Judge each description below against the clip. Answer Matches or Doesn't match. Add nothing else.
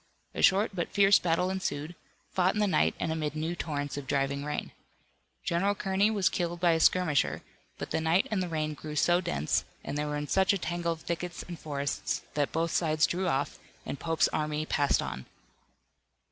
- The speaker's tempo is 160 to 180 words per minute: Doesn't match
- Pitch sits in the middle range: Matches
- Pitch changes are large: Doesn't match